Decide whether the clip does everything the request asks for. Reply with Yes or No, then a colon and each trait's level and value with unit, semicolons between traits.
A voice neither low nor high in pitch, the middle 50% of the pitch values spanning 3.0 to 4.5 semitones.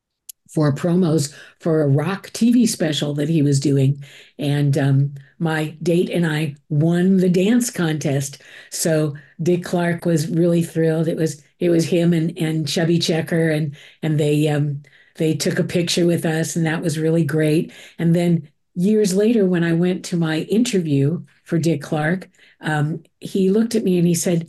No: medium, 165 Hz; narrow, 2.4 semitones